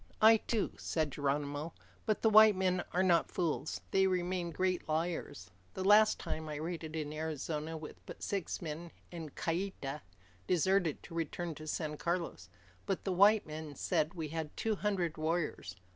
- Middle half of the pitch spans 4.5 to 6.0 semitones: No, average, 3.3 semitones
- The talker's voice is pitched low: No, medium, 165 Hz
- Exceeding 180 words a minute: No, average, 165 wpm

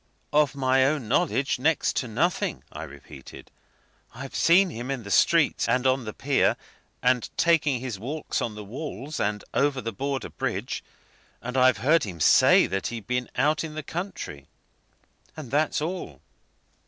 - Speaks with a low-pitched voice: Yes, low, 130 Hz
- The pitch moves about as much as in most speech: Yes, average, 4.7 semitones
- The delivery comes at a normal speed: Yes, average, 165 wpm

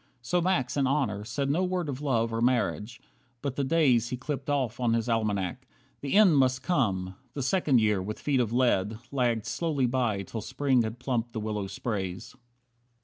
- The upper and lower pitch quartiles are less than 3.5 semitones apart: No, average, 4.0 semitones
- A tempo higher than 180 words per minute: Yes, average, 190 wpm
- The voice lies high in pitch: No, low, 125 Hz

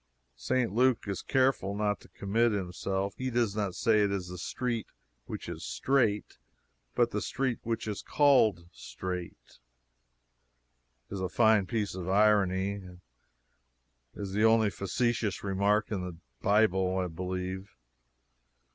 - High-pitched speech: No, low, 100 Hz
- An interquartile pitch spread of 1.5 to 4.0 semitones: Yes, average, 3.1 semitones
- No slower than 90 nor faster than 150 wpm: Yes, average, 140 wpm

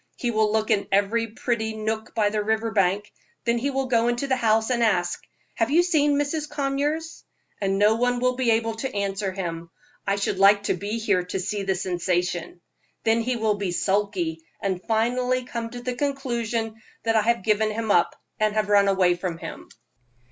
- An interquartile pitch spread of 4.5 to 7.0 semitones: No, average, 3.3 semitones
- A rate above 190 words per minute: Yes, average, 200 wpm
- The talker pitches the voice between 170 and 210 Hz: No, high, 220 Hz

